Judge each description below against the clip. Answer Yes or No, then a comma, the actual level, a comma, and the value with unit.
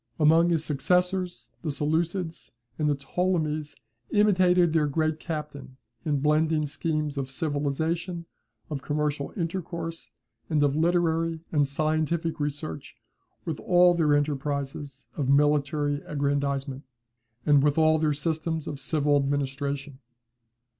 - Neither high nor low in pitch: Yes, medium, 150 Hz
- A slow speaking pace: Yes, slow, 120 wpm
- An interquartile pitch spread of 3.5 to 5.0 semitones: No, narrow, 2.5 semitones